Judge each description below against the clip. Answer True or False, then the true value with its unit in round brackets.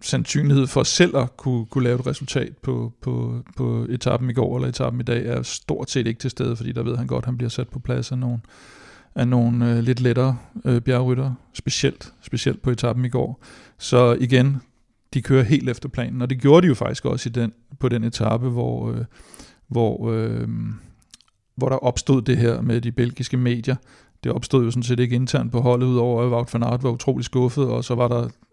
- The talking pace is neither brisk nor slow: True (215 wpm)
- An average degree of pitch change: False (1.6 semitones)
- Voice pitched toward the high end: False (125 Hz)